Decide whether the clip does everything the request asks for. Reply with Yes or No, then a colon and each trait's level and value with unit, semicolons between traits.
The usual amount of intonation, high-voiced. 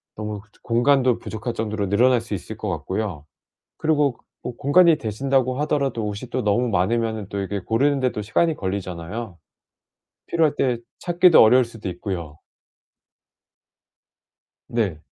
No: average, 4.6 semitones; low, 115 Hz